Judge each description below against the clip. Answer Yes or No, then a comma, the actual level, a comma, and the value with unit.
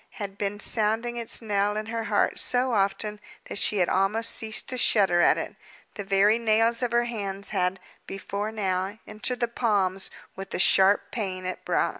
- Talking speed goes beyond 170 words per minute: Yes, average, 185 wpm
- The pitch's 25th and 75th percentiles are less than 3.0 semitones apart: Yes, narrow, 2.6 semitones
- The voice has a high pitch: Yes, high, 210 Hz